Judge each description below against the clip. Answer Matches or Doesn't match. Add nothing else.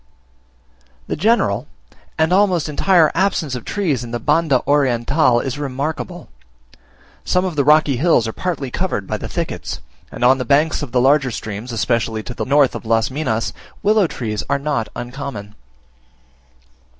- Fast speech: Doesn't match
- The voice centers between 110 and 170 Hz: Matches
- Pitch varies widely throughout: Doesn't match